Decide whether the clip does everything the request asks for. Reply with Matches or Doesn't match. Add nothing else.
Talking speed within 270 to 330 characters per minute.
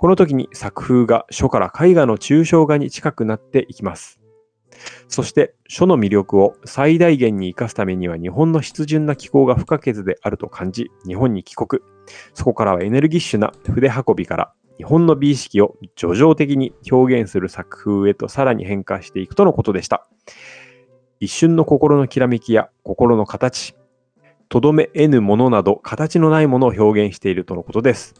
Doesn't match